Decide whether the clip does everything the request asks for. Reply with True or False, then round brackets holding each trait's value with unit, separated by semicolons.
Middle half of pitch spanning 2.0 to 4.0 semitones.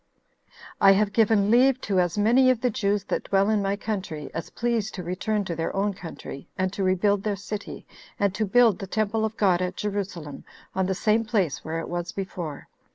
True (2.9 semitones)